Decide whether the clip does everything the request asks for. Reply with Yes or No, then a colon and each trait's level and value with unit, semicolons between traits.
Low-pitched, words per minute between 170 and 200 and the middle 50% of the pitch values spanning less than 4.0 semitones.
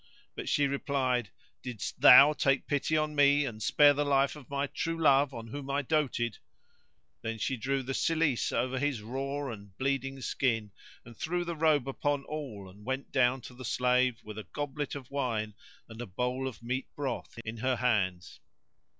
Yes: low, 130 Hz; average, 185 wpm; average, 3.3 semitones